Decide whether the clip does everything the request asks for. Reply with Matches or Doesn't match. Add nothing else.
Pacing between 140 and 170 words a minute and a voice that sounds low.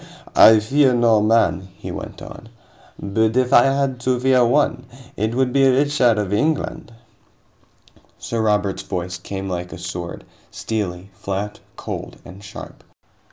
Matches